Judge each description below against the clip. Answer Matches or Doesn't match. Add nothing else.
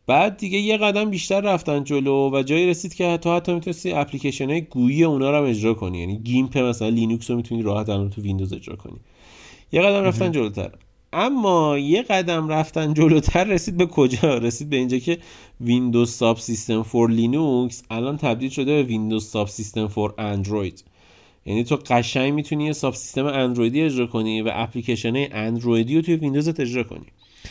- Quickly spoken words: Matches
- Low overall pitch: Matches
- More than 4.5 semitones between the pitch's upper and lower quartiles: Matches